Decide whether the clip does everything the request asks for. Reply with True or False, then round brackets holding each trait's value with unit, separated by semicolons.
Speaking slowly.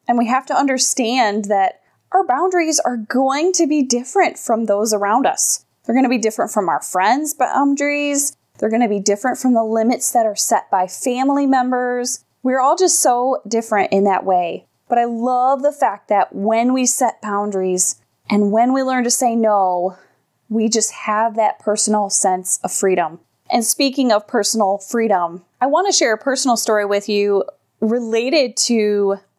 False (175 wpm)